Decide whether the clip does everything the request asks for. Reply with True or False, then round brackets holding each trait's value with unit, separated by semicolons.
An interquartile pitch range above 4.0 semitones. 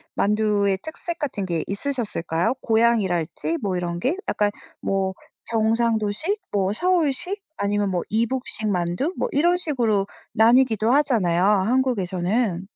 True (5.3 semitones)